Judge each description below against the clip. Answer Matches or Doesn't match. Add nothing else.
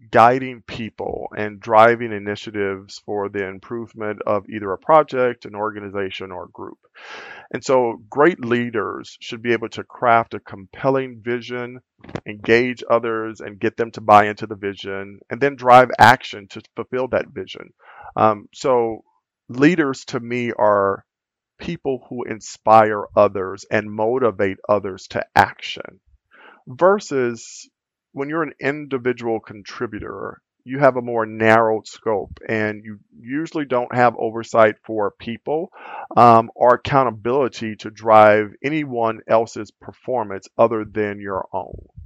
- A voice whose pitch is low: Matches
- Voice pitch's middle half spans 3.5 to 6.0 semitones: Doesn't match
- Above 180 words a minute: Doesn't match